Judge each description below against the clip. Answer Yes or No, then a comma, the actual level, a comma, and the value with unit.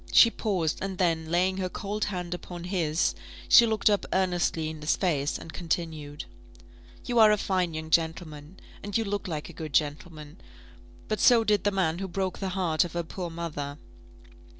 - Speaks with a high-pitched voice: No, medium, 175 Hz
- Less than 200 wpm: Yes, average, 185 wpm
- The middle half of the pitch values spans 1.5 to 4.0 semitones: Yes, average, 3.4 semitones